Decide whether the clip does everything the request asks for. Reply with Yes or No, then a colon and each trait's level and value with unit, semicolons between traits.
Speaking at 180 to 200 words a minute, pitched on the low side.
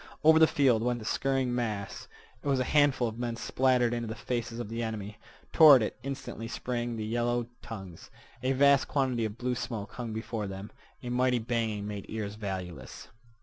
Yes: average, 190 wpm; low, 120 Hz